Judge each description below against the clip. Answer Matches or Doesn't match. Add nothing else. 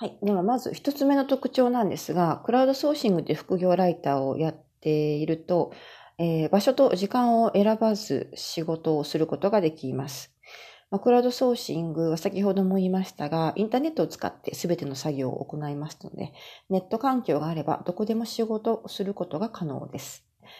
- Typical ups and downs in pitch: Doesn't match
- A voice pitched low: Doesn't match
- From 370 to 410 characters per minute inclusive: Matches